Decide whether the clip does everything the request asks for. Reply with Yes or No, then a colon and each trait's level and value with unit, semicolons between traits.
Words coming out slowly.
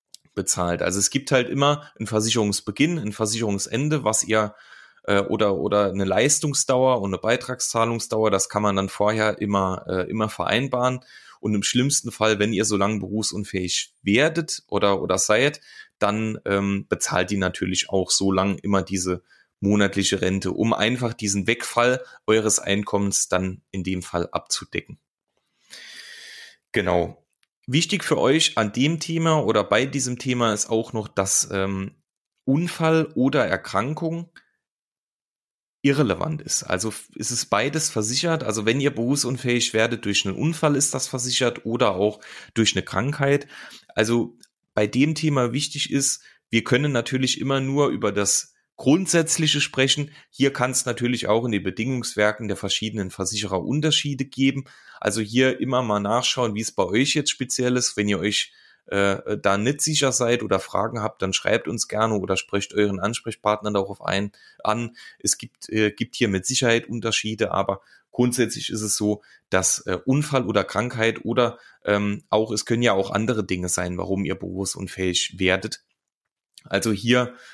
No: average, 155 wpm